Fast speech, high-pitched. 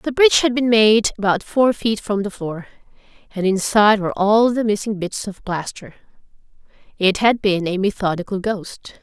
No: average, 175 wpm; high, 210 Hz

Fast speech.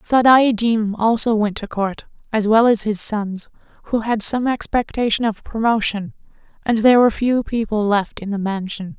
No: average, 165 wpm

